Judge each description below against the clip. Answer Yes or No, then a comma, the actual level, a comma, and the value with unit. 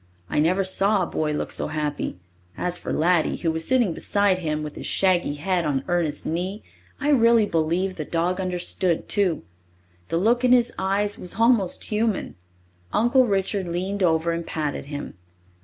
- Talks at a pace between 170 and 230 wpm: Yes, average, 175 wpm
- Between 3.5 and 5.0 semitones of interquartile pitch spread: Yes, average, 3.9 semitones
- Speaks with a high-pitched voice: No, medium, 180 Hz